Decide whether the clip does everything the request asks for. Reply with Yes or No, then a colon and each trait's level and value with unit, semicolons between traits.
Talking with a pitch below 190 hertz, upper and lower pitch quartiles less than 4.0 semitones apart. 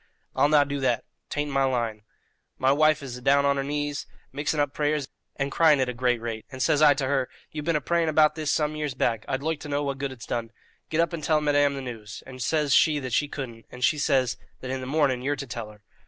Yes: medium, 140 Hz; average, 2.7 semitones